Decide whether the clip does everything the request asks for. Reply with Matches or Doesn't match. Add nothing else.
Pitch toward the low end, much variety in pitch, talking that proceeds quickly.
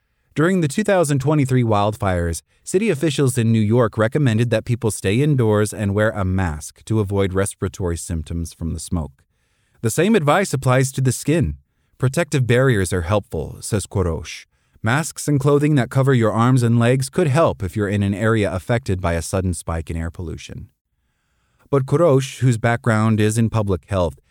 Doesn't match